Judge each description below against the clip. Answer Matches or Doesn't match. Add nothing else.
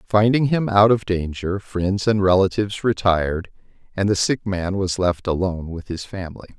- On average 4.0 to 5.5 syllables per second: Matches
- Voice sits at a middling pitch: Doesn't match